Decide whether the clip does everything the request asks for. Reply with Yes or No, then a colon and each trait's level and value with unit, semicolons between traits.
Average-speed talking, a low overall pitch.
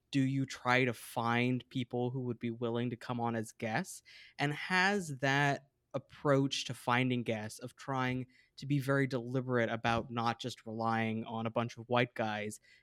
Yes: average, 180 wpm; low, 125 Hz